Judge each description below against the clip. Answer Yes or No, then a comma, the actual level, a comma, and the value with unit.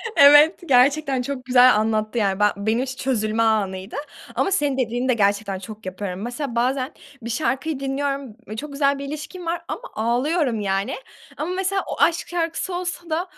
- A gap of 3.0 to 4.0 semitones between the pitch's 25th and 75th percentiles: No, wide, 5.5 semitones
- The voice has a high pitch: Yes, very high, 255 Hz